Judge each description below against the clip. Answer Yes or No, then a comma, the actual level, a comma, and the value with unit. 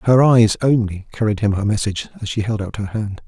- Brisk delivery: Yes, fast, 240 wpm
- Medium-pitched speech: No, low, 110 Hz